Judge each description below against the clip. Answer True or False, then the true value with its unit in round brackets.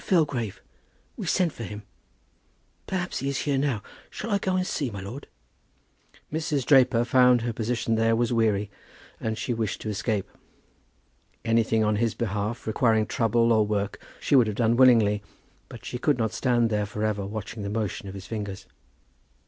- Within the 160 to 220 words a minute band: True (180 wpm)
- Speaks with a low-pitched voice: True (115 Hz)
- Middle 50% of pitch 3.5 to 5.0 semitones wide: False (3.0 semitones)